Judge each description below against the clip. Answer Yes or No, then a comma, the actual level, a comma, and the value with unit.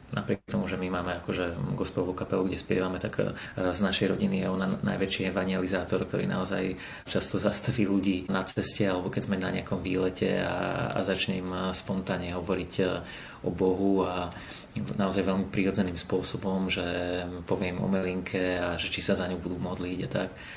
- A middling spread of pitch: No, narrow, 1.3 semitones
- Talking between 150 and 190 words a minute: Yes, fast, 165 wpm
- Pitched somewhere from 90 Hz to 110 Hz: Yes, very low, 95 Hz